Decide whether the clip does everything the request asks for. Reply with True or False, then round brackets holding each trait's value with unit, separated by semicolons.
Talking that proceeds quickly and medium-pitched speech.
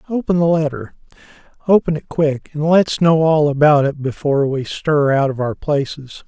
False (170 wpm; 150 Hz)